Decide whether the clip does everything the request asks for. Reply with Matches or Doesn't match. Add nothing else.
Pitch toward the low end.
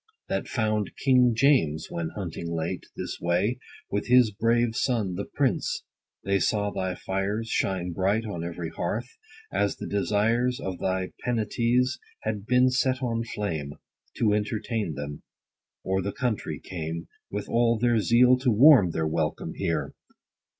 Matches